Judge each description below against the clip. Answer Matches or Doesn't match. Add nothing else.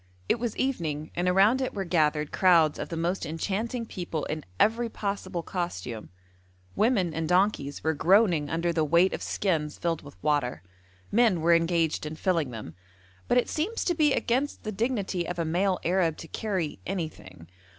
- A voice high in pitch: Doesn't match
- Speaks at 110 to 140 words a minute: Doesn't match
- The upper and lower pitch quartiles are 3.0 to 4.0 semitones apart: Doesn't match